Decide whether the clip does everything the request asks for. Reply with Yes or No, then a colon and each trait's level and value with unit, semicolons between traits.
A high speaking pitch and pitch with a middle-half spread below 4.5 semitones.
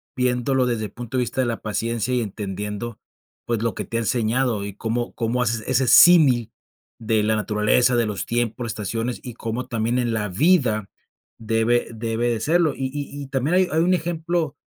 No: low, 120 Hz; average, 2.7 semitones